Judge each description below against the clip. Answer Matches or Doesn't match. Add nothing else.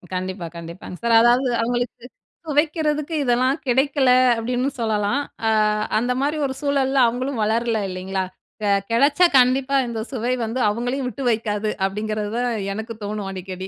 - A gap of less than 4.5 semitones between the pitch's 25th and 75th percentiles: Matches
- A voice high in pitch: Matches